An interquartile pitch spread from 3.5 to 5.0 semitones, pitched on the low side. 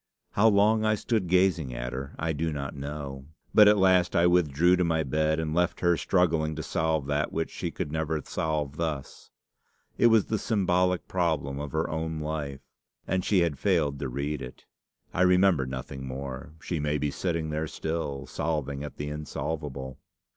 Yes: average, 3.8 semitones; very low, 80 Hz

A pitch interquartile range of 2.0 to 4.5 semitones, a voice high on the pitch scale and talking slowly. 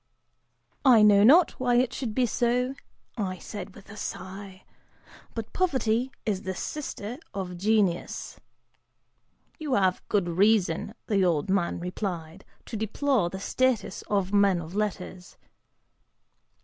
Yes: average, 4.2 semitones; high, 205 Hz; slow, 130 wpm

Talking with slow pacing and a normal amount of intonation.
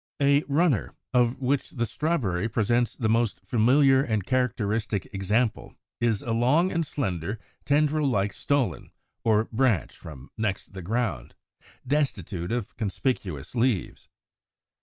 Yes: slow, 125 wpm; average, 4.7 semitones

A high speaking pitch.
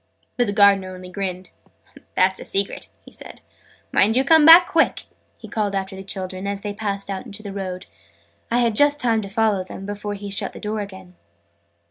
Yes: high, 200 Hz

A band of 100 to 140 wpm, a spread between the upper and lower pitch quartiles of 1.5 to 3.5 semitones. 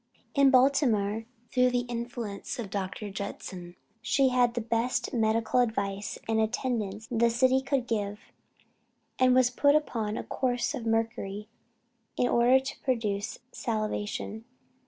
Yes: slow, 135 wpm; average, 3.0 semitones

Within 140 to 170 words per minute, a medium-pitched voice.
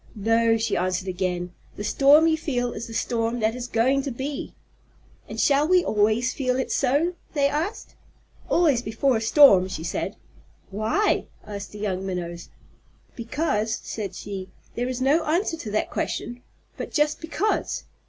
No: average, 165 wpm; high, 235 Hz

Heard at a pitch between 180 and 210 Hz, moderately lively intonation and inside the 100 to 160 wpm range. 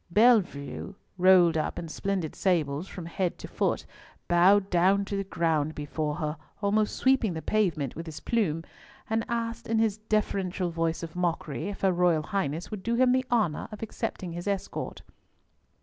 No: medium, 185 Hz; average, 4.3 semitones; average, 170 wpm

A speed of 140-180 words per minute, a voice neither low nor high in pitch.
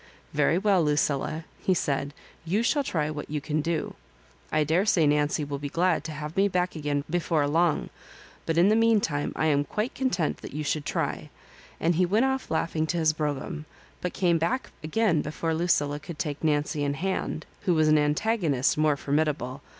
No: average, 190 wpm; medium, 155 Hz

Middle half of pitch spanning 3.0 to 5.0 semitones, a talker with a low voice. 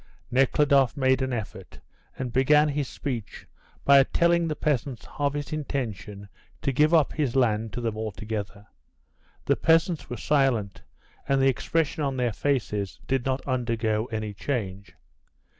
Yes: average, 4.5 semitones; low, 130 Hz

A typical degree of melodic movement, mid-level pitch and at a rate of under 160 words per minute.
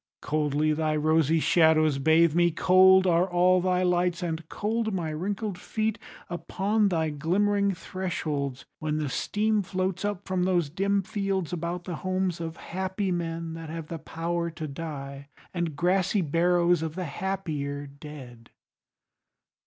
Yes: average, 3.1 semitones; medium, 170 Hz; average, 145 wpm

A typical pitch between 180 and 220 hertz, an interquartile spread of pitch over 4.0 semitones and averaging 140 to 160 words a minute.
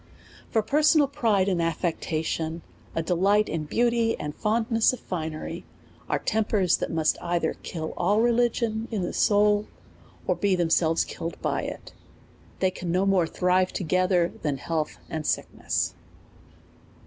Yes: medium, 185 Hz; average, 4.9 semitones; average, 145 wpm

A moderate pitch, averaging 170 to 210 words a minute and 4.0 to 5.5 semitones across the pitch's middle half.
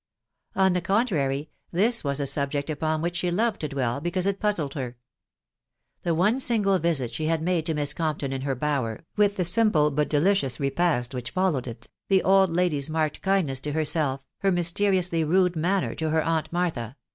Yes: medium, 160 Hz; average, 195 wpm; average, 4.7 semitones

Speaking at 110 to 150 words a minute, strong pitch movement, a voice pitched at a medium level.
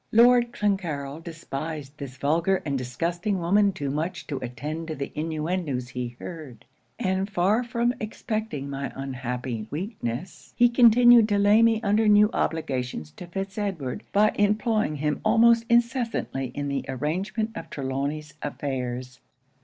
Yes: average, 140 wpm; wide, 7.4 semitones; medium, 165 Hz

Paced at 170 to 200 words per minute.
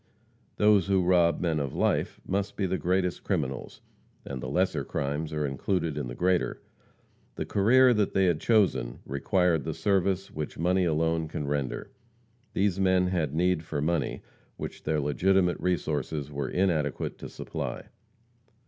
No: average, 150 wpm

